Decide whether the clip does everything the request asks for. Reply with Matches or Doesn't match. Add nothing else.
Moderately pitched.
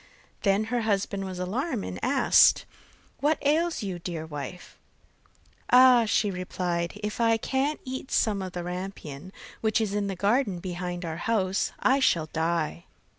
Doesn't match